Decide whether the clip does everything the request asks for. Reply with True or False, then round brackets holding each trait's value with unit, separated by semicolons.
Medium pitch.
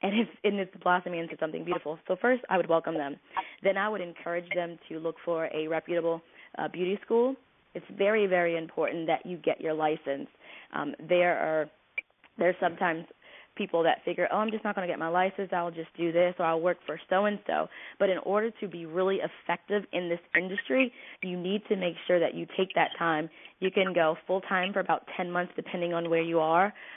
True (175 Hz)